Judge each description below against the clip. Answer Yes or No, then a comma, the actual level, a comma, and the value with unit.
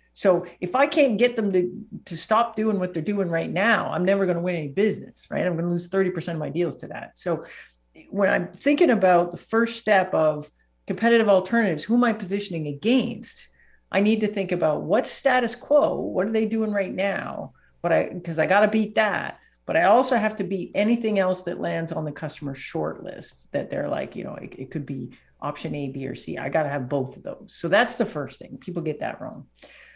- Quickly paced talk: Yes, fast, 230 wpm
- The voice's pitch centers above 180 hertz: Yes, high, 190 Hz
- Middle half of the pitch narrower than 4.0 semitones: No, average, 4.8 semitones